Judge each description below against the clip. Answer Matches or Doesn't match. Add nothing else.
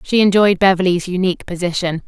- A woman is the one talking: Matches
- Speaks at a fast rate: Doesn't match